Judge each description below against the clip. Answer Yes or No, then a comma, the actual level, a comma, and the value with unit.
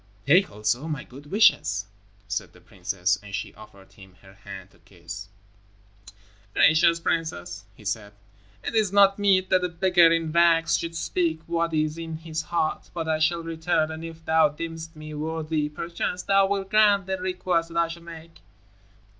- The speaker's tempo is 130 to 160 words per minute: No, average, 175 wpm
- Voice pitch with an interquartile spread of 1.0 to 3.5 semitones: Yes, narrow, 2.6 semitones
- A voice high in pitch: No, medium, 165 Hz